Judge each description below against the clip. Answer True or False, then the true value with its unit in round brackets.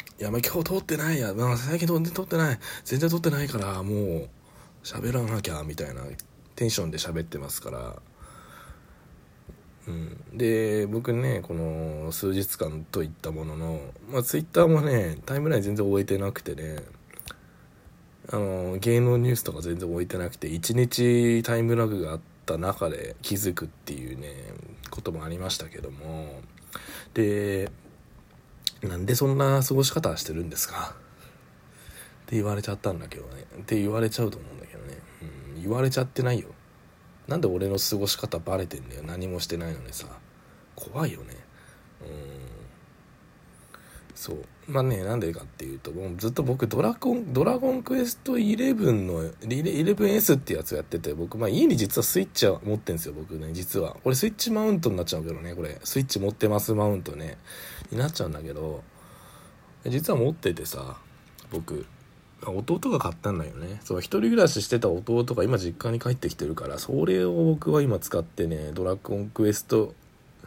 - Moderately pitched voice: False (105 Hz)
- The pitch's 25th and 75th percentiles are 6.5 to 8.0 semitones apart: True (6.8 semitones)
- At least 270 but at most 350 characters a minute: True (345 characters per minute)